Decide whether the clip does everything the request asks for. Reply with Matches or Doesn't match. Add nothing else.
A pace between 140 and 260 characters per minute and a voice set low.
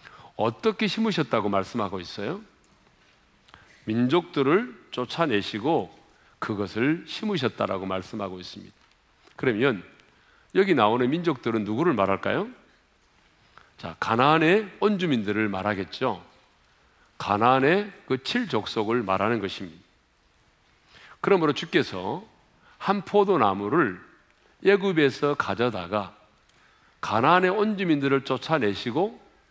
Matches